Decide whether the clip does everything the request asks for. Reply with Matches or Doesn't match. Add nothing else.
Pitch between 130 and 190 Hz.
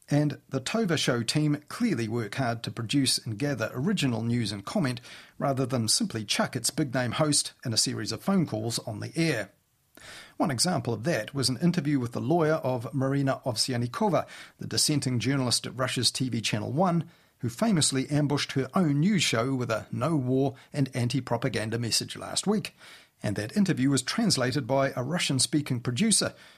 Matches